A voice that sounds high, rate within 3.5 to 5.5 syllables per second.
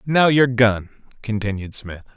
No: low, 115 Hz; 4.4 syllables/s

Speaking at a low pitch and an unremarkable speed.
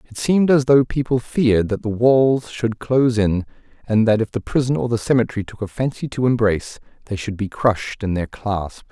No: low, 115 Hz; fast, 215 wpm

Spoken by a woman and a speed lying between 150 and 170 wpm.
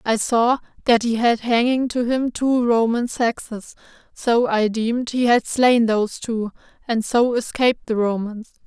Yes: female; average, 165 wpm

